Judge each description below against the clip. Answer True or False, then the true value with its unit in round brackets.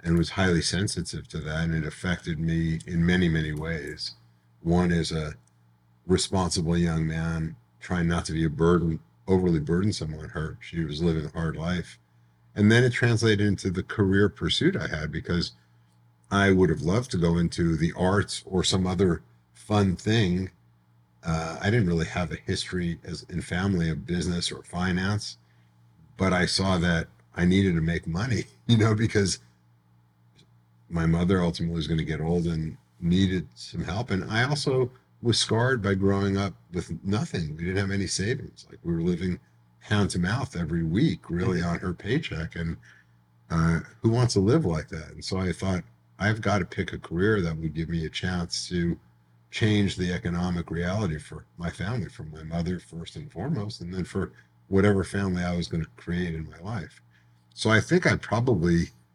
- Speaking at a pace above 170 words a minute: True (185 wpm)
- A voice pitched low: True (85 Hz)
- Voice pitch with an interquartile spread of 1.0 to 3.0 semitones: False (3.4 semitones)